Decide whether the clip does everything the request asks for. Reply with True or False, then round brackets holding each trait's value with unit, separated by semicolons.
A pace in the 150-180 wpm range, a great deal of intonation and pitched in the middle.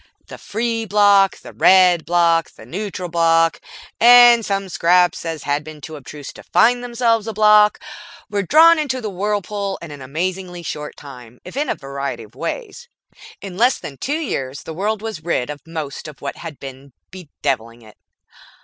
True (175 wpm; 6.2 semitones; 180 Hz)